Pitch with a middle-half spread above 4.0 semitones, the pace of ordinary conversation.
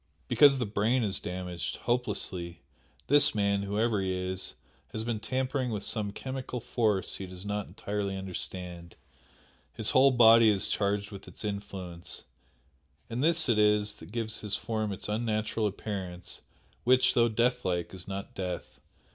No: average, 3.6 semitones; average, 155 wpm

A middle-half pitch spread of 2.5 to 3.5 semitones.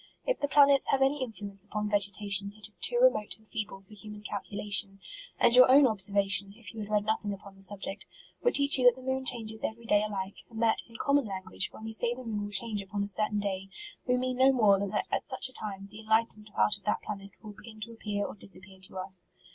Yes: average, 2.8 semitones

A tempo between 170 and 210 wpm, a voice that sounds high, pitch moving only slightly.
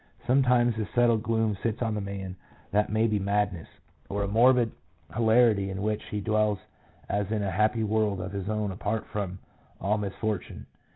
No: average, 180 wpm; low, 105 Hz; narrow, 1.9 semitones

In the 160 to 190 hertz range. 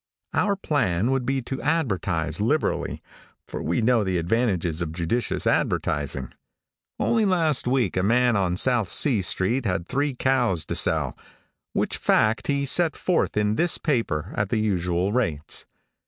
No: low, 110 Hz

